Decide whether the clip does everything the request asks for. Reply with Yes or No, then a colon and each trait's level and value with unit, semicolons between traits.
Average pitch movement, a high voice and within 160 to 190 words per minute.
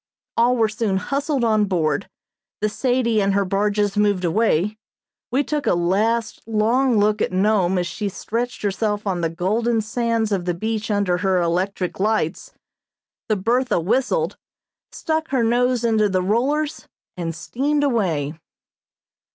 No: average, 3.9 semitones; high, 215 Hz; average, 150 wpm